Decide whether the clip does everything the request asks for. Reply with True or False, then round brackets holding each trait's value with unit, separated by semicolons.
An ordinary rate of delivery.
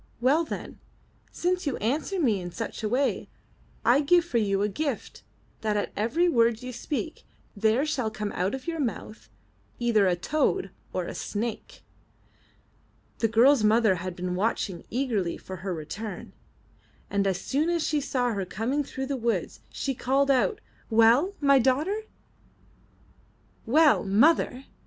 True (150 wpm)